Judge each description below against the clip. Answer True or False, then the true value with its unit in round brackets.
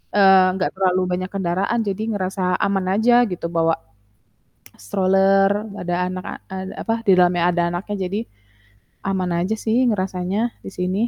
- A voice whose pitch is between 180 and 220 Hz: True (190 Hz)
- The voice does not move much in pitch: True (1.4 semitones)